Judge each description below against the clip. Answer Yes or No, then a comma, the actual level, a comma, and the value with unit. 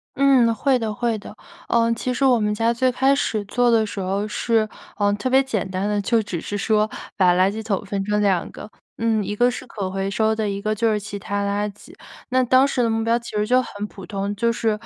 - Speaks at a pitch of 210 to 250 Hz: Yes, high, 215 Hz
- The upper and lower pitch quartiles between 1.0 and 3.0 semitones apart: Yes, narrow, 2.6 semitones